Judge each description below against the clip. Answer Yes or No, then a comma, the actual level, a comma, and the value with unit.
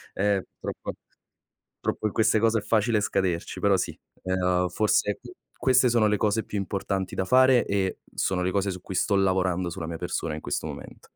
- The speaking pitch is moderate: No, low, 100 Hz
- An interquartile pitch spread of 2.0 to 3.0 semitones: Yes, average, 2.7 semitones